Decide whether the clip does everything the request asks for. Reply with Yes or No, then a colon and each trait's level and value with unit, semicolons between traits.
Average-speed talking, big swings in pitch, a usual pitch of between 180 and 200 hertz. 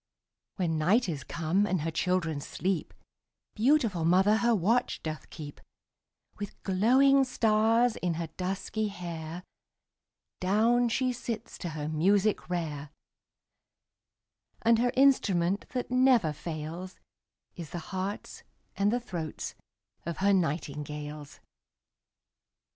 No: slow, 115 wpm; wide, 5.7 semitones; medium, 185 Hz